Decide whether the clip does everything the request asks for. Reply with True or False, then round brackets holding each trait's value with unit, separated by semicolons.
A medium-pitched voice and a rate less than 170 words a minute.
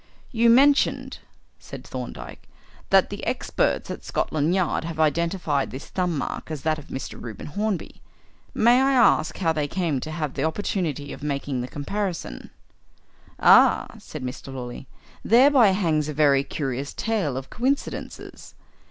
True (155 Hz; 150 wpm)